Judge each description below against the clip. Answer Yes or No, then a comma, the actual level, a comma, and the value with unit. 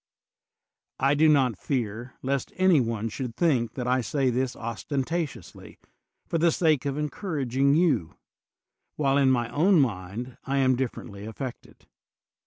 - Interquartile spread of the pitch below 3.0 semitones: No, average, 3.7 semitones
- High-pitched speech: No, low, 130 Hz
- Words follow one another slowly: No, average, 150 wpm